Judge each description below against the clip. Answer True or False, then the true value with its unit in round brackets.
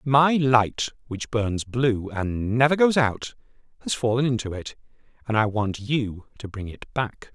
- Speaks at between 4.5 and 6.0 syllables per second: False (4.0 syllables/s)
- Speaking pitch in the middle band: False (120 Hz)